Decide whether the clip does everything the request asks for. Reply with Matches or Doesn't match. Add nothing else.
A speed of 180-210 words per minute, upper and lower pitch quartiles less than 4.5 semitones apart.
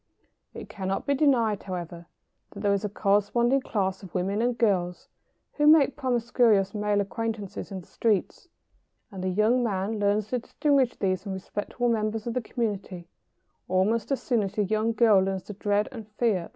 Matches